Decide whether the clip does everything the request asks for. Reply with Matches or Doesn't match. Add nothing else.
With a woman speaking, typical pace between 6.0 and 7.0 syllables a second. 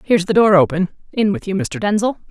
Matches